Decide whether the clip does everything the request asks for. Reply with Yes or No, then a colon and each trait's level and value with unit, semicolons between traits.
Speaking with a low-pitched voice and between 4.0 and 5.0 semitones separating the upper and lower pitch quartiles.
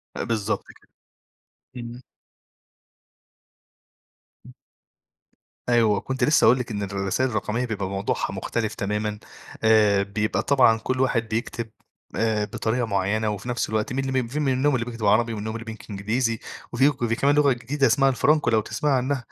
No: low, 115 Hz; average, 3.3 semitones